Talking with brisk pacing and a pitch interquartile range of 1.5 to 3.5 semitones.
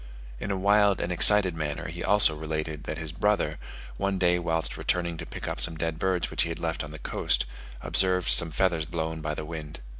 Yes: fast, 215 wpm; average, 2.8 semitones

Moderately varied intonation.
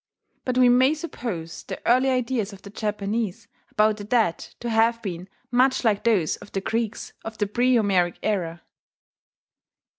Yes: average, 3.6 semitones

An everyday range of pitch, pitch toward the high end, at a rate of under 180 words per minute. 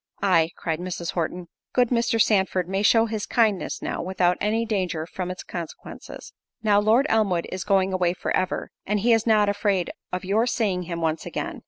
No: average, 3.3 semitones; high, 195 Hz; average, 185 wpm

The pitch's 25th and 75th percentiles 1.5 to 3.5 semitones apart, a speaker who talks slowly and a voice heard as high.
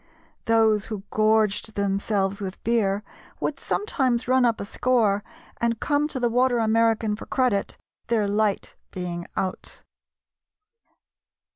Yes: average, 2.9 semitones; slow, 125 wpm; high, 220 Hz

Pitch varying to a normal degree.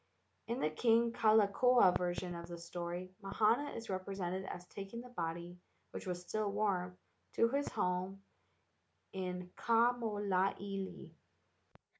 Yes: average, 3.7 semitones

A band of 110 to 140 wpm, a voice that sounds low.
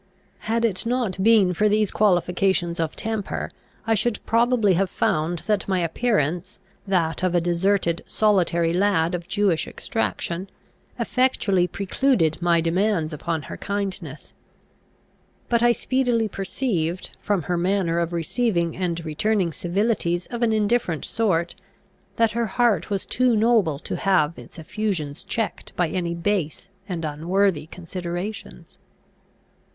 No: slow, 135 wpm; medium, 185 Hz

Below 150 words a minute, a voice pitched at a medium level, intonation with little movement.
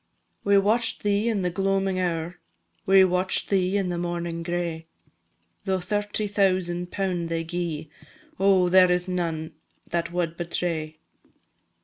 Yes: slow, 135 wpm; medium, 180 Hz; narrow, 2.2 semitones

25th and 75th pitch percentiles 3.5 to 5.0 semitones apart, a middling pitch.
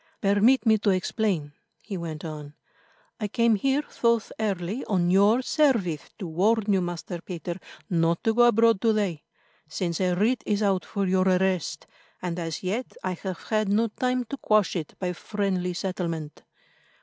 No: average, 3.9 semitones; high, 195 Hz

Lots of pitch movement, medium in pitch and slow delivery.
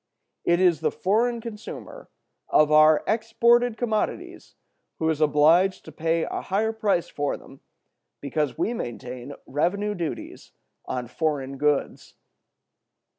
Yes: wide, 6.5 semitones; medium, 165 Hz; slow, 125 wpm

